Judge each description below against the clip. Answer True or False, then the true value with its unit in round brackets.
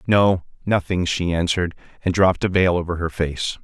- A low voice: True (90 Hz)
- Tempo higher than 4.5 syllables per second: True (5.4 syllables/s)